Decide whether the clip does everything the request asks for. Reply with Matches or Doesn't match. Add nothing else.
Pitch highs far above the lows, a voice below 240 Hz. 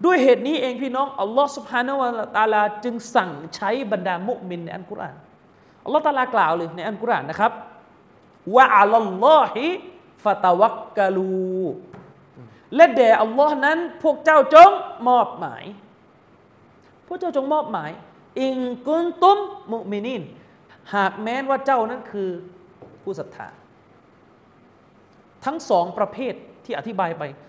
Doesn't match